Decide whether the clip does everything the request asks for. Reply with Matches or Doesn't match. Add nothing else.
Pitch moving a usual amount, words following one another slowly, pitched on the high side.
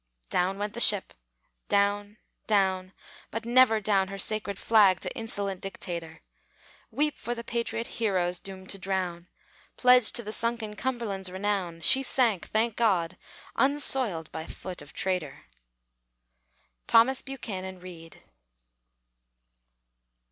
Matches